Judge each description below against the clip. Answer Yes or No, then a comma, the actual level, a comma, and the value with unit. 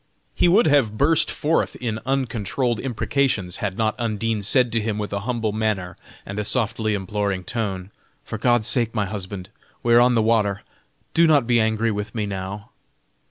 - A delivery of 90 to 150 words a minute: No, average, 180 wpm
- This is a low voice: Yes, low, 110 Hz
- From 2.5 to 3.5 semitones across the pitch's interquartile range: Yes, average, 2.9 semitones